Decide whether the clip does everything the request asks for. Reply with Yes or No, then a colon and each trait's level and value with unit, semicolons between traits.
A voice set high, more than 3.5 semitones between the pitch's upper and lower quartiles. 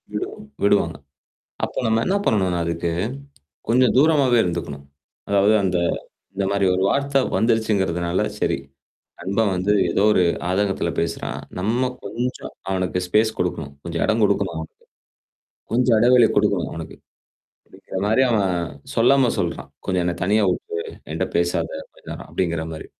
No: low, 100 Hz; average, 4.6 semitones